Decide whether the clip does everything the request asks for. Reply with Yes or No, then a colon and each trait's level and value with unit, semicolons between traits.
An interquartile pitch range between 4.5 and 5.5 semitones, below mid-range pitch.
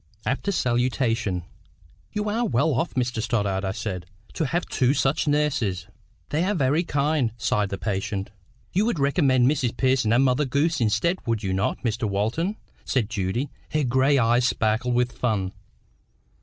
Yes: average, 5.1 semitones; low, 125 Hz